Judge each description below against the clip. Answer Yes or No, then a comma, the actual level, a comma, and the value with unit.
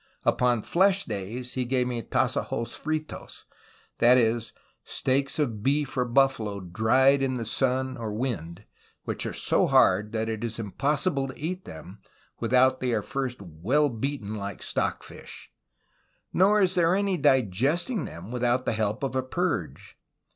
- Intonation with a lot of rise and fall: No, average, 3.9 semitones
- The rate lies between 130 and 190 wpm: Yes, average, 155 wpm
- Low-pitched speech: Yes, low, 125 Hz